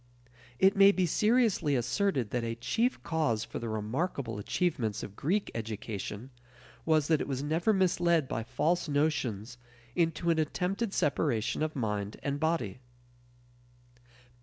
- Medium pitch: Yes, medium, 150 Hz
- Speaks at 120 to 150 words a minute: Yes, slow, 135 wpm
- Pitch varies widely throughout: Yes, wide, 7.2 semitones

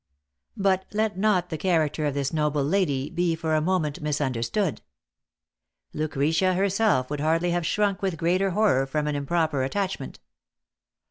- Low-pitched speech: No, medium, 165 Hz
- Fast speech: No, average, 145 wpm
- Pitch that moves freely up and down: No, average, 4.3 semitones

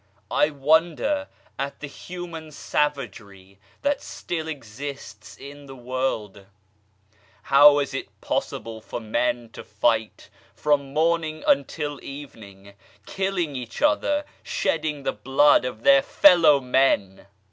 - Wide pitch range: No, average, 5.0 semitones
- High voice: No, medium, 140 Hz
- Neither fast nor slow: No, slow, 115 wpm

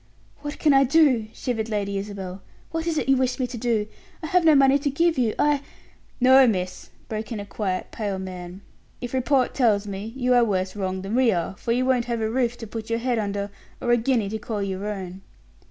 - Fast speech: Yes, fast, 235 wpm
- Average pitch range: Yes, average, 4.5 semitones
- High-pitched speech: Yes, high, 230 Hz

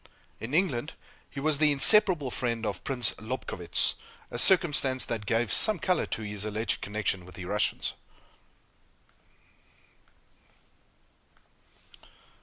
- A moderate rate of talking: No, slow, 110 wpm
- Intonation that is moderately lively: No, wide, 6.0 semitones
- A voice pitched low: Yes, low, 120 Hz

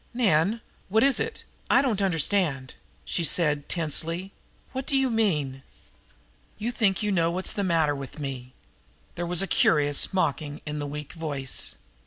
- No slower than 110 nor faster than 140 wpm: No, average, 160 wpm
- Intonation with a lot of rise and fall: Yes, wide, 5.7 semitones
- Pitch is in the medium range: Yes, medium, 170 Hz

